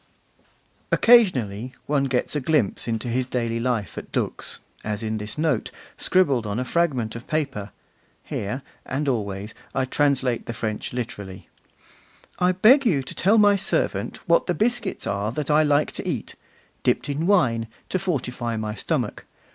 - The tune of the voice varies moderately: No, wide, 5.8 semitones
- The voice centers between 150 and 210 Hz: No, low, 130 Hz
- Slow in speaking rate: No, average, 160 wpm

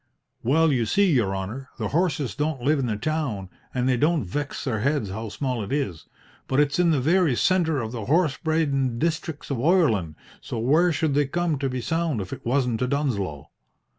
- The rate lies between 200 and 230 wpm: Yes, fast, 205 wpm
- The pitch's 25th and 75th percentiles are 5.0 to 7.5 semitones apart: Yes, average, 5.3 semitones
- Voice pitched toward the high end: No, low, 135 Hz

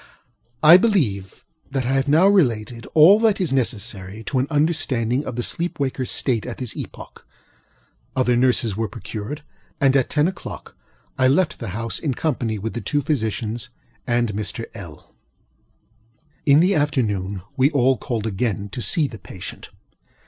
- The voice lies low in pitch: Yes, low, 125 Hz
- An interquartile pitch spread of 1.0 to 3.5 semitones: No, average, 4.9 semitones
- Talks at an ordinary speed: Yes, average, 160 wpm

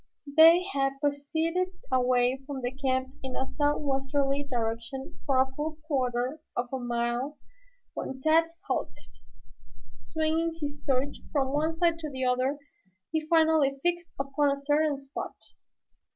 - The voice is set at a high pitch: Yes, very high, 280 Hz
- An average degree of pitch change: Yes, average, 3.1 semitones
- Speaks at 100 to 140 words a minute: Yes, slow, 135 wpm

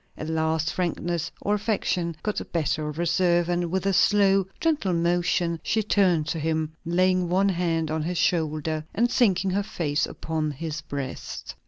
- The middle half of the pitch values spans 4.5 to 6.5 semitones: No, average, 2.9 semitones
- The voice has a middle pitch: Yes, medium, 170 Hz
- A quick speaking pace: No, average, 170 wpm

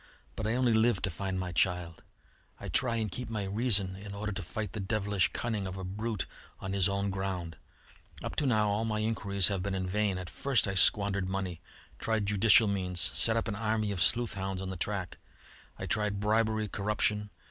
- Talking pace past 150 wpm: Yes, average, 200 wpm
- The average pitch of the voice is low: Yes, low, 100 Hz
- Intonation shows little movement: Yes, narrow, 2.3 semitones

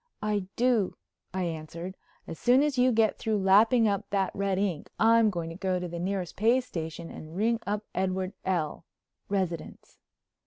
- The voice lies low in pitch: No, high, 195 Hz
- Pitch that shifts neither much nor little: Yes, average, 3.8 semitones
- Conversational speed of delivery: Yes, average, 170 wpm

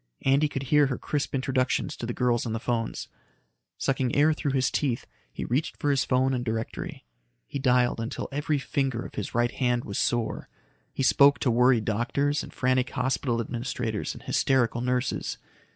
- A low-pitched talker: Yes, low, 125 Hz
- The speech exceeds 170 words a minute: Yes, average, 180 wpm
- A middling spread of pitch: No, narrow, 2.3 semitones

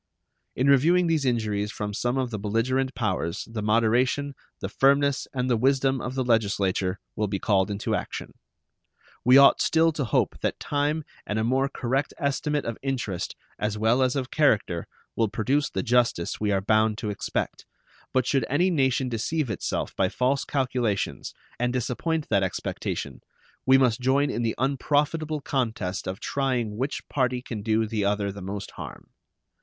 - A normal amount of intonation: Yes, average, 4.3 semitones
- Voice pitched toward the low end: Yes, low, 125 Hz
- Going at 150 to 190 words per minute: Yes, average, 170 wpm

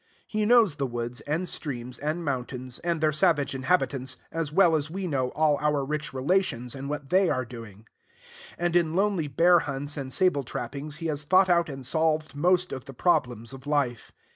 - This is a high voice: No, medium, 150 Hz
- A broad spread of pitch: No, average, 4.5 semitones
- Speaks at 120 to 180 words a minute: No, average, 190 wpm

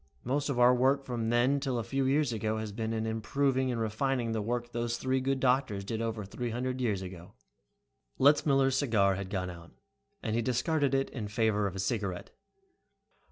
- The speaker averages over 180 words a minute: Yes, average, 195 wpm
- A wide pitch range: No, average, 3.6 semitones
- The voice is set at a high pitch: No, low, 120 Hz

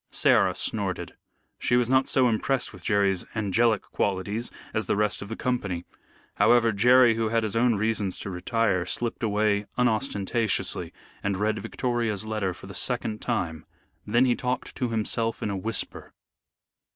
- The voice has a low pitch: Yes, low, 110 Hz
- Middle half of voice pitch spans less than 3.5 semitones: Yes, average, 2.8 semitones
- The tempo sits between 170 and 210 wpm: No, average, 160 wpm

